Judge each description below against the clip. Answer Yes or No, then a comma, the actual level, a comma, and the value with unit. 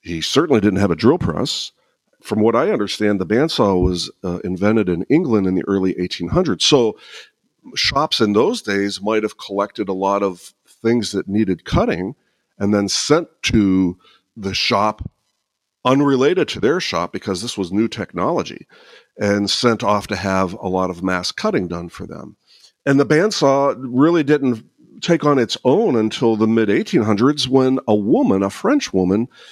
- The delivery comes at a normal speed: Yes, average, 170 wpm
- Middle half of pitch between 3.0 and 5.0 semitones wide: Yes, average, 4.0 semitones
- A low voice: Yes, low, 105 Hz